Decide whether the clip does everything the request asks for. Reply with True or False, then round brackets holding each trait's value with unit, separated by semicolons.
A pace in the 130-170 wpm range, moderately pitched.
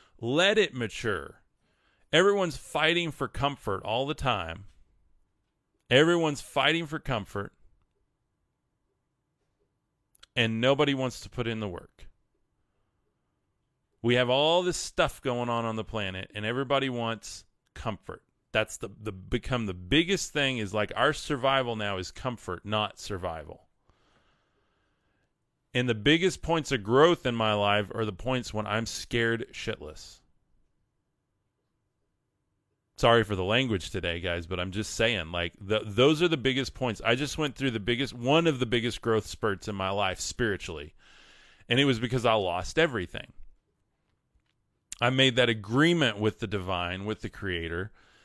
False (145 wpm; 115 Hz)